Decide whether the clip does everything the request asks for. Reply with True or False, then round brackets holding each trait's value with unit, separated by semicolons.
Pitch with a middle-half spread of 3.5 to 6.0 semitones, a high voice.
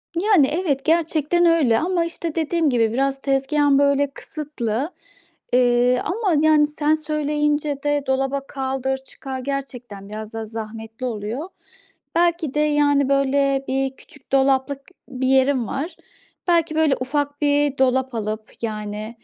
False (3.0 semitones; 275 Hz)